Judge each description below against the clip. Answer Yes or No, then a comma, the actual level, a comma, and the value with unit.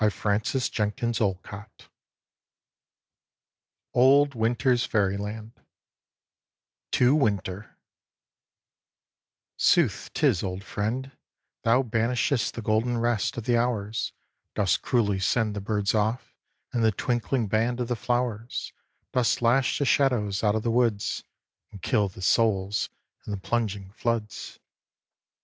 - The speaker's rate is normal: No, slow, 115 wpm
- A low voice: Yes, low, 110 Hz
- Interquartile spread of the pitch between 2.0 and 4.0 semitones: Yes, average, 2.8 semitones